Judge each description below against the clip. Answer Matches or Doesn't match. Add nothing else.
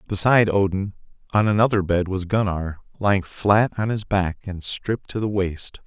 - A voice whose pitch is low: Matches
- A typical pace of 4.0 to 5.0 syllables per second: Matches